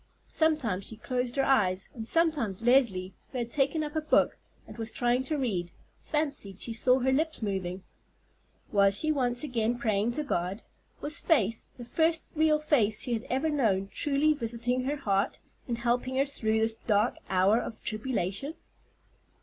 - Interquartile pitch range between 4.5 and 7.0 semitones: Yes, average, 4.9 semitones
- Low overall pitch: No, high, 240 Hz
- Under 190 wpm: Yes, average, 170 wpm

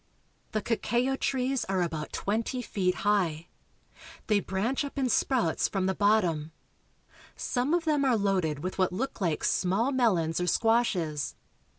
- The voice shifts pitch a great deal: Yes, wide, 5.8 semitones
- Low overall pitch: No, high, 205 Hz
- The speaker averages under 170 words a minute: Yes, average, 150 wpm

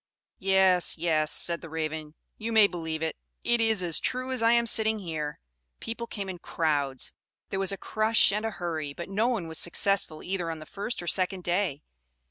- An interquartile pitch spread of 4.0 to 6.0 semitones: Yes, average, 5.1 semitones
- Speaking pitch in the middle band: Yes, medium, 180 Hz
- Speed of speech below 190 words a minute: No, average, 200 wpm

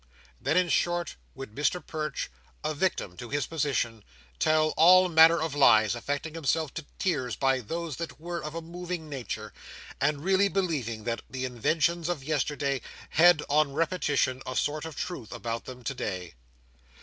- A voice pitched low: No, medium, 150 Hz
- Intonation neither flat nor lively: Yes, average, 4.4 semitones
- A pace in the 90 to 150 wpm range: No, average, 160 wpm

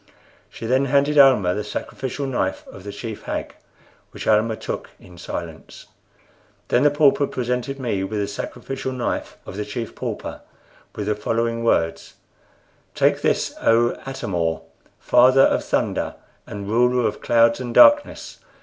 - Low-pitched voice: Yes, low, 115 Hz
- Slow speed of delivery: No, average, 150 wpm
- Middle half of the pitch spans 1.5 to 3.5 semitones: No, average, 4.1 semitones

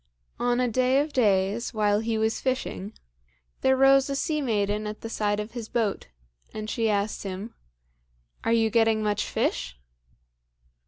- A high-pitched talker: Yes, high, 220 Hz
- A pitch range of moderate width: Yes, average, 3.0 semitones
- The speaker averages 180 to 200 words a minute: No, average, 160 wpm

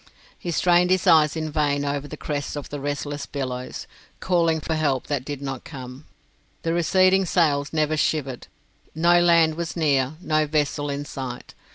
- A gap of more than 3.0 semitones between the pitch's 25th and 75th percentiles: No, narrow, 2.5 semitones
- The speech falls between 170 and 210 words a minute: Yes, average, 175 wpm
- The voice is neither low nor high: Yes, medium, 150 Hz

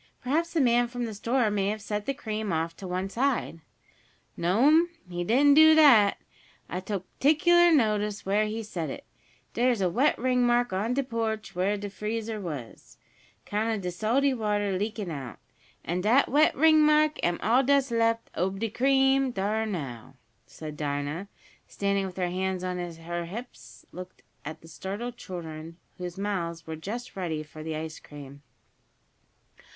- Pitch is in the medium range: No, high, 205 Hz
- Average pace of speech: Yes, average, 165 wpm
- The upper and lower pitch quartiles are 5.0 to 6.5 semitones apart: Yes, wide, 5.6 semitones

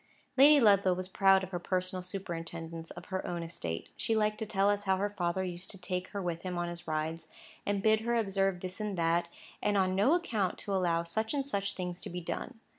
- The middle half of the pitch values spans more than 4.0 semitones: No, average, 2.8 semitones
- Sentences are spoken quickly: Yes, fast, 230 wpm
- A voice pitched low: No, medium, 185 Hz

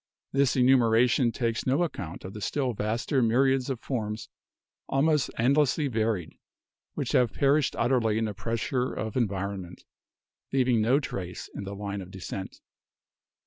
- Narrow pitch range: No, average, 4.1 semitones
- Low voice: Yes, low, 115 Hz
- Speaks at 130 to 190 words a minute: Yes, average, 145 wpm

